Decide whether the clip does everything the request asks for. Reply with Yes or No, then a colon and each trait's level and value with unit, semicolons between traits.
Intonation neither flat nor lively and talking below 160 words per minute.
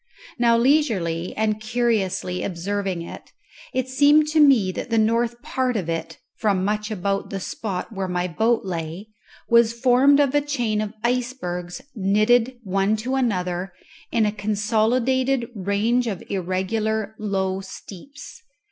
Yes: average, 4.2 semitones; average, 140 wpm